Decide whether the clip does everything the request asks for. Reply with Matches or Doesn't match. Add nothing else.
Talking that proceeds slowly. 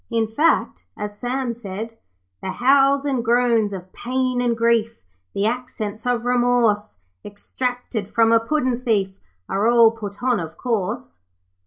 Doesn't match